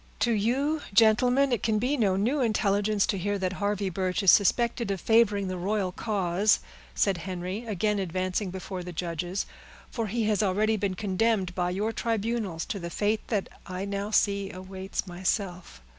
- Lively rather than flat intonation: No, average, 2.8 semitones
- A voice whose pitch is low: No, high, 200 Hz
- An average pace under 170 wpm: No, average, 175 wpm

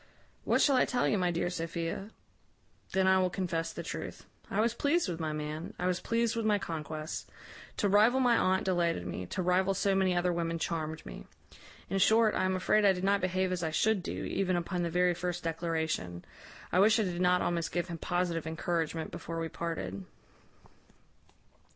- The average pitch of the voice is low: No, medium, 180 Hz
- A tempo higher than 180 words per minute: Yes, average, 200 wpm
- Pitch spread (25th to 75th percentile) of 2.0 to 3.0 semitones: Yes, average, 2.7 semitones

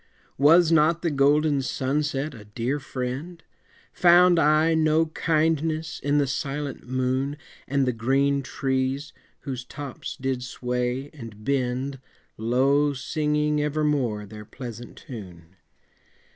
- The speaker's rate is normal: No, slow, 115 wpm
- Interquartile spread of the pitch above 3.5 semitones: No, average, 3.1 semitones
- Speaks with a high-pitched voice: No, medium, 140 Hz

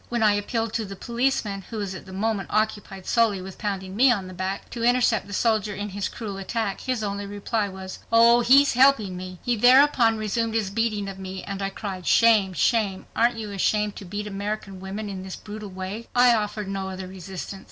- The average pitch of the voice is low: No, high, 205 Hz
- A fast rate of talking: Yes, fast, 215 wpm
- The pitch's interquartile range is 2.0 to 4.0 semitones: Yes, average, 2.9 semitones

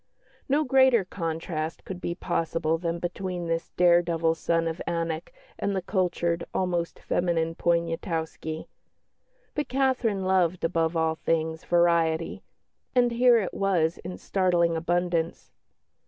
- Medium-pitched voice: Yes, medium, 170 Hz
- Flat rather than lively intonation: Yes, narrow, 2.1 semitones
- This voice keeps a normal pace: No, slow, 125 wpm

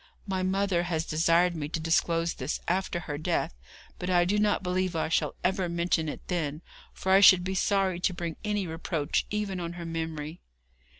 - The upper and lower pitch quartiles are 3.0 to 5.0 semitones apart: No, narrow, 2.4 semitones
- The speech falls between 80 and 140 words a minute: No, average, 190 wpm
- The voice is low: No, medium, 175 Hz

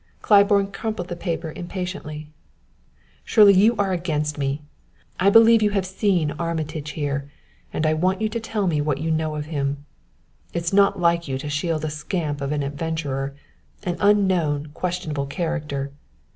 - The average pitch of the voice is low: No, medium, 165 Hz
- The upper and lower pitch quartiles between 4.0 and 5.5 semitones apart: Yes, average, 4.3 semitones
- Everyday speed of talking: Yes, average, 165 wpm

